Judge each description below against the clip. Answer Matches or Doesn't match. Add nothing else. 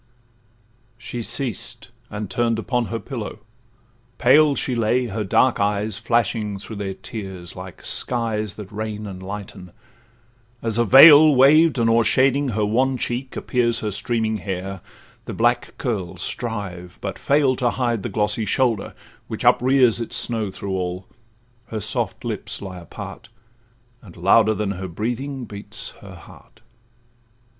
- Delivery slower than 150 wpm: Matches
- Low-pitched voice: Matches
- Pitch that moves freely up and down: Doesn't match